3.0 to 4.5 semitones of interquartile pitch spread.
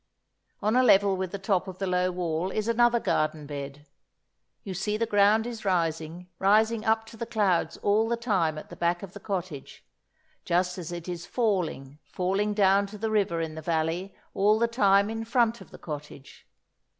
Yes: average, 4.2 semitones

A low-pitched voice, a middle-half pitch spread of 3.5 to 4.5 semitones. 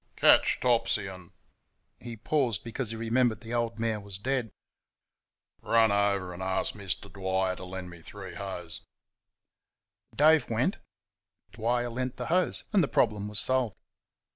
Yes: low, 110 Hz; average, 4.1 semitones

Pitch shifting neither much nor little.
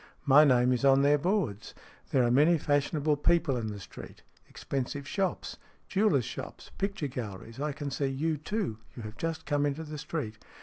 Yes: average, 3.9 semitones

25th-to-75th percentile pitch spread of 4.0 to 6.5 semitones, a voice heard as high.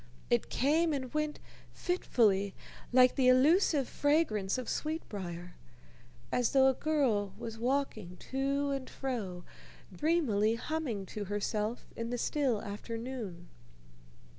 Yes: wide, 5.4 semitones; high, 245 Hz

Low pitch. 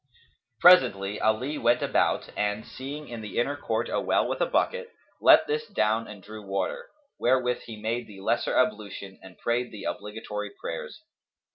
Yes: low, 110 Hz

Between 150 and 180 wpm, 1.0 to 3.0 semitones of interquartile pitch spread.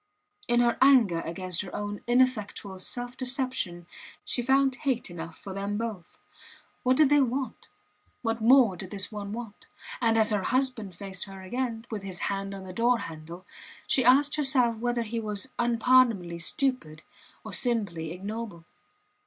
No: average, 160 wpm; average, 4.8 semitones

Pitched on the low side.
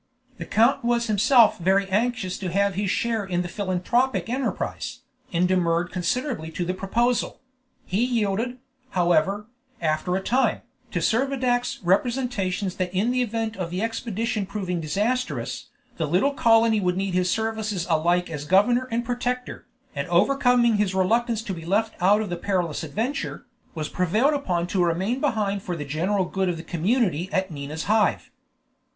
No: high, 200 Hz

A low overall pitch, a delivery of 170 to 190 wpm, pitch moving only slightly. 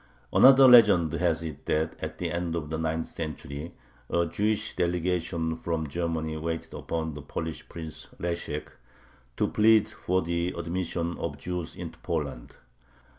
No: very low, 85 Hz; average, 145 wpm; narrow, 1.9 semitones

